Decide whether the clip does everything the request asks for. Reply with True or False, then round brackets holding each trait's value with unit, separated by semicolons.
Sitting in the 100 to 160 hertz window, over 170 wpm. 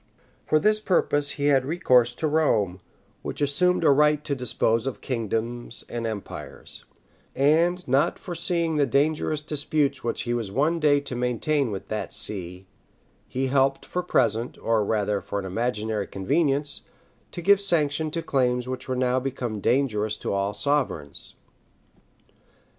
False (135 Hz; 150 wpm)